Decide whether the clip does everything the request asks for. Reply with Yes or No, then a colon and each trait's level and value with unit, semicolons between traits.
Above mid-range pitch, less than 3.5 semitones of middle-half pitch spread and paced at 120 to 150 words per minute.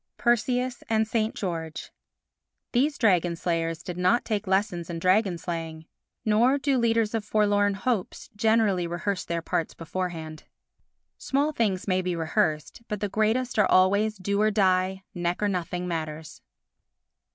No: high, 195 Hz; average, 4.1 semitones; average, 145 wpm